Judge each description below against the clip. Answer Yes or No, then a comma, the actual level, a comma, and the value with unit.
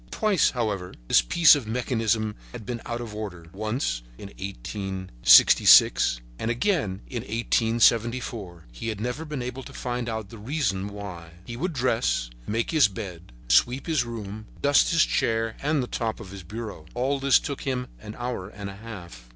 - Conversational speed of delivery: Yes, average, 170 wpm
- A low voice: Yes, low, 115 Hz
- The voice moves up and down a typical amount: Yes, average, 4.1 semitones